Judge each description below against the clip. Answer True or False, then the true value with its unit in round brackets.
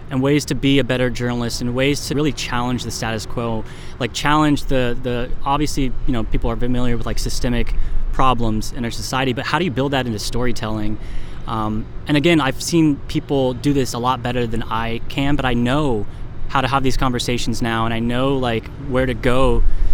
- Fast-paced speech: True (210 wpm)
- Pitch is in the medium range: False (125 Hz)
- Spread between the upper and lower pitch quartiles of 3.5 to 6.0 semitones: False (2.8 semitones)